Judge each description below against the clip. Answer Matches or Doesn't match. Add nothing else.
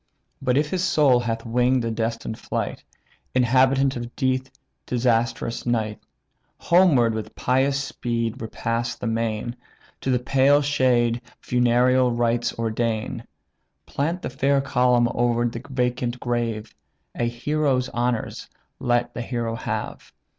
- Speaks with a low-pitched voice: Matches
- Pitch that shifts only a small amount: Matches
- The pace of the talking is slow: Matches